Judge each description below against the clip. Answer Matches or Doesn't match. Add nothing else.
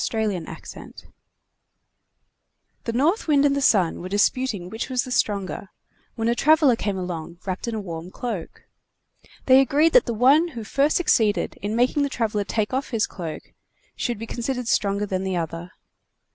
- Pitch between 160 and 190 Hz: Doesn't match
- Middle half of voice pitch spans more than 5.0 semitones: Matches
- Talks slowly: Doesn't match